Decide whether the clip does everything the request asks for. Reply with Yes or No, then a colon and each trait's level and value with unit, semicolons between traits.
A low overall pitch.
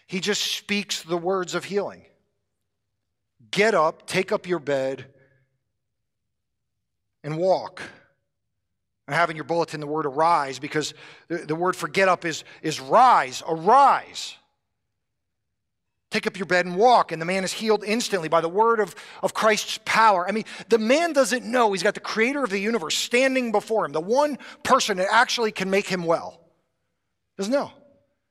No: medium, 175 Hz